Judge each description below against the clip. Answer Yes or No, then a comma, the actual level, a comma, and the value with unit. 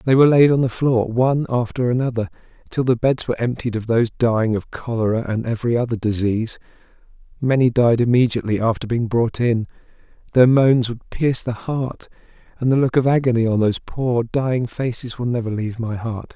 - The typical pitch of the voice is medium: No, low, 120 Hz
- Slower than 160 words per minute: No, average, 180 wpm